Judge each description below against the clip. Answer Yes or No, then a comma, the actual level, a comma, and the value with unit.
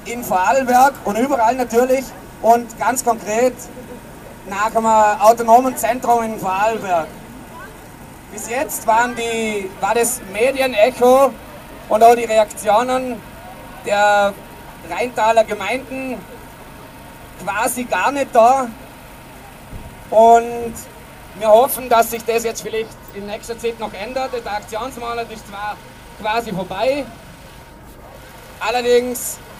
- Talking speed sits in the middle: No, slow, 105 wpm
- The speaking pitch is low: No, high, 230 Hz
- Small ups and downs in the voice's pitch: Yes, narrow, 2.3 semitones